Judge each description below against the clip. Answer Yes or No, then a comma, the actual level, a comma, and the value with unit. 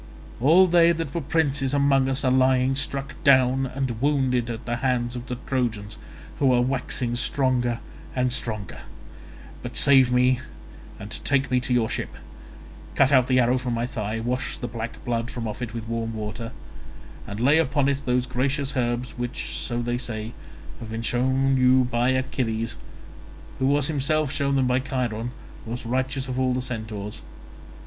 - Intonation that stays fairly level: Yes, narrow, 2.1 semitones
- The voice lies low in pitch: Yes, low, 125 Hz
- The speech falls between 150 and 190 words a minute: Yes, average, 175 wpm